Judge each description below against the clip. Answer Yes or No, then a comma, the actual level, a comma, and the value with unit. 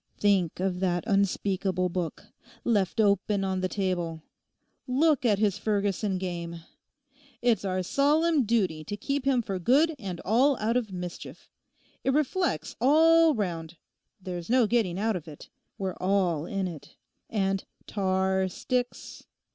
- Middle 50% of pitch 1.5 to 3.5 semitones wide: No, average, 4.7 semitones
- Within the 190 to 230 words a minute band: No, average, 140 wpm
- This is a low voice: No, high, 195 Hz